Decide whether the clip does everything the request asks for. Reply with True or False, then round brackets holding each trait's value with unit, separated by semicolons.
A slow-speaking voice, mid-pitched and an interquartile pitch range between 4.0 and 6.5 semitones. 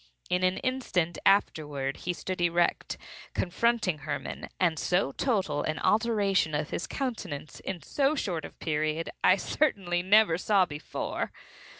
True (130 wpm; 180 Hz; 4.8 semitones)